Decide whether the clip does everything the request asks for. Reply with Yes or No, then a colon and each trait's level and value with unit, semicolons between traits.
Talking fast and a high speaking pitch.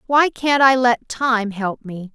No: average, 195 wpm; high, 240 Hz